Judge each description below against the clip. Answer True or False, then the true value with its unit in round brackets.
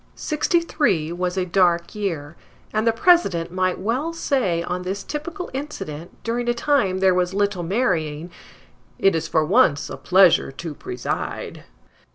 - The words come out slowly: False (155 wpm)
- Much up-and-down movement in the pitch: True (5.9 semitones)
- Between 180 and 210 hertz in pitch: True (190 Hz)